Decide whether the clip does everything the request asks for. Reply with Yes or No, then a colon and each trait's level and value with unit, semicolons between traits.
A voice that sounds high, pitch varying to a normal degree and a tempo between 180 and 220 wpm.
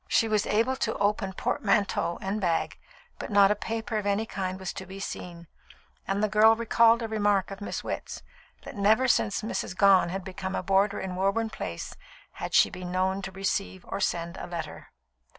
No: high, 195 Hz; narrow, 2.2 semitones; average, 195 wpm